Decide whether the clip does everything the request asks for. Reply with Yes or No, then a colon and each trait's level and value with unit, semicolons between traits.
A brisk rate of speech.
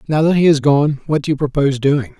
Yes: fast, 275 wpm